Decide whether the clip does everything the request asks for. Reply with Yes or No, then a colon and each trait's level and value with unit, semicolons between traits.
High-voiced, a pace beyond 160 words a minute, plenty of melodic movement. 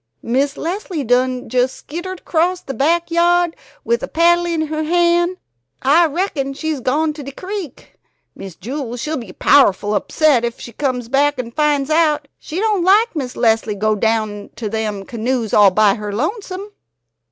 Yes: very high, 285 Hz; average, 170 wpm; wide, 6.4 semitones